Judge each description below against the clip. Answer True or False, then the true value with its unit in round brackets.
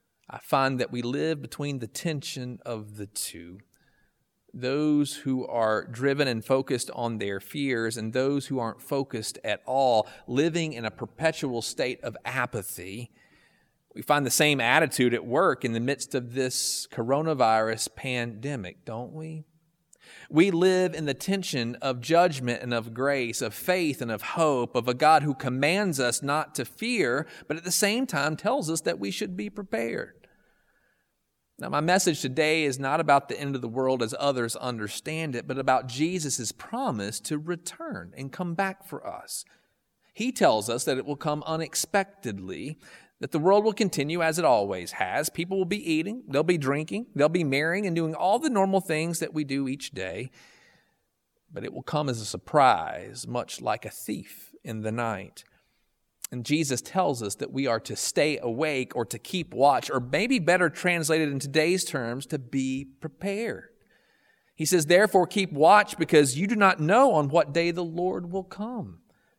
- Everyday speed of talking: True (180 wpm)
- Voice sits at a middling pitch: True (145 Hz)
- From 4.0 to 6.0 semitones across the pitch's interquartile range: True (5.1 semitones)